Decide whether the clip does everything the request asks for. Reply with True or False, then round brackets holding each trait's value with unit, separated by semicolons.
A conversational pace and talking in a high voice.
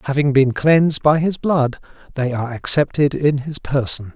False (175 wpm; 140 Hz)